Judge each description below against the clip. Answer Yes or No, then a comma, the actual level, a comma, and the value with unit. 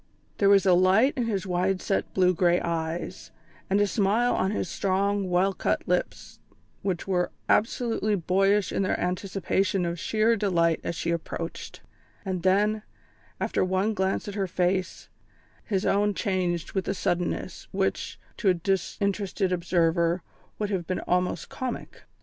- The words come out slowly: No, average, 155 wpm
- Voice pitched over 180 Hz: Yes, high, 190 Hz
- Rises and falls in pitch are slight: Yes, narrow, 2.2 semitones